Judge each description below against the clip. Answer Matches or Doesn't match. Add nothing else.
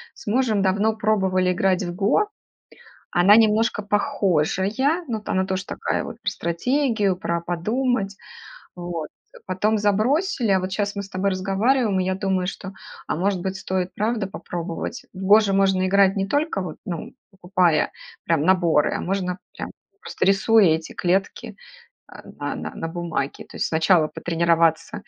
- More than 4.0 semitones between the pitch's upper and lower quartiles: Doesn't match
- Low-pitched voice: Doesn't match